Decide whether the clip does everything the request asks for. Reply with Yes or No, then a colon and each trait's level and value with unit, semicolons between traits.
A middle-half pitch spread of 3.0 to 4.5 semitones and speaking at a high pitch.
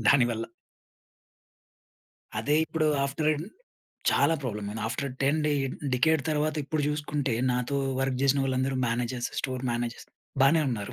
No: average, 3.6 semitones; low, 135 Hz